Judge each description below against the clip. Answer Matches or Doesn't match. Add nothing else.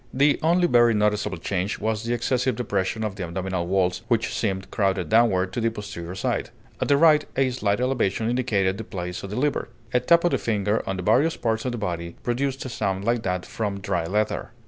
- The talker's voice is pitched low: Matches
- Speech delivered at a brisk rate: Matches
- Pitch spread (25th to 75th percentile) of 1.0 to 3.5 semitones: Doesn't match